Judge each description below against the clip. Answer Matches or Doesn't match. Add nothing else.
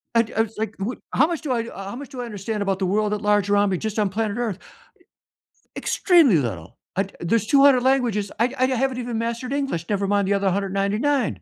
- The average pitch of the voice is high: Matches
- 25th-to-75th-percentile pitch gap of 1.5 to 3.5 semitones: Doesn't match